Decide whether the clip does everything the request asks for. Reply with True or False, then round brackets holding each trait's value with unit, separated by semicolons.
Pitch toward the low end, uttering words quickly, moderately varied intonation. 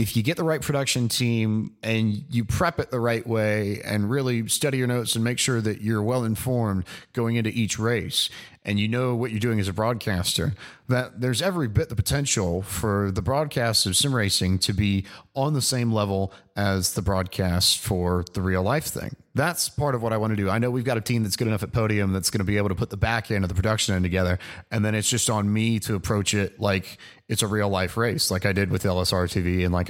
True (110 Hz; 245 wpm; 3.4 semitones)